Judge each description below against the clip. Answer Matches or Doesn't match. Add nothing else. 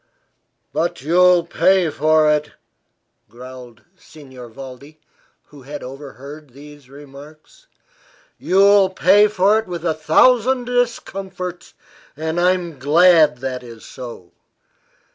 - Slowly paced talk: Matches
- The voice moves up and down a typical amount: Matches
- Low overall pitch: Doesn't match